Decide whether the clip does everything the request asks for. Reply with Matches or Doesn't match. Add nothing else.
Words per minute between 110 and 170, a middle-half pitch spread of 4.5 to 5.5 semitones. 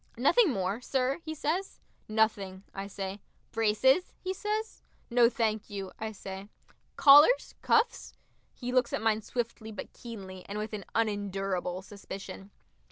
Matches